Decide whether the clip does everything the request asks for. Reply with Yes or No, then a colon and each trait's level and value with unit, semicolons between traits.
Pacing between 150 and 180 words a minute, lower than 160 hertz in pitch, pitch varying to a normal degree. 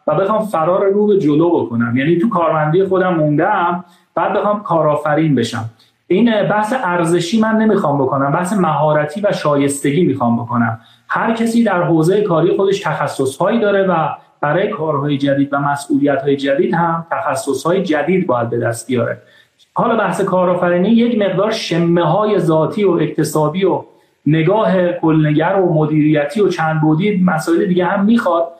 No: fast, 155 wpm; medium, 170 Hz; average, 4.7 semitones